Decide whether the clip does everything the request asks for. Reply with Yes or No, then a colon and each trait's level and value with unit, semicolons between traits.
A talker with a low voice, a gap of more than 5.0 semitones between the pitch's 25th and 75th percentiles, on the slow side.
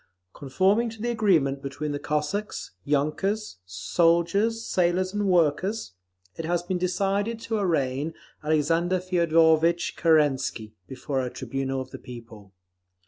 No: medium, 165 Hz; wide, 5.5 semitones; slow, 125 wpm